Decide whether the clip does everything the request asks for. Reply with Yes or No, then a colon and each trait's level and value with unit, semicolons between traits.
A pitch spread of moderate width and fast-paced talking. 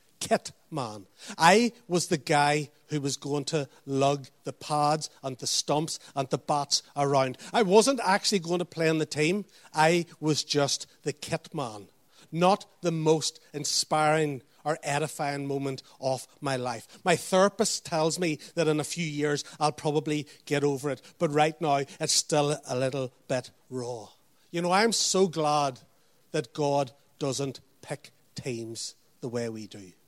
No: average, 3.0 semitones; average, 165 wpm